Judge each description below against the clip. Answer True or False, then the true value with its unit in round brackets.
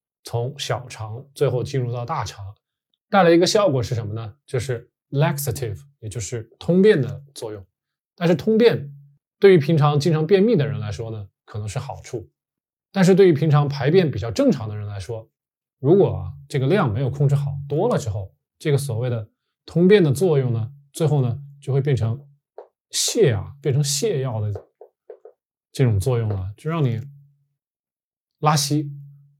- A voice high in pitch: False (140 Hz)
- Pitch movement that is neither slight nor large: True (4.3 semitones)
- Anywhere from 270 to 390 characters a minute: False (255 characters per minute)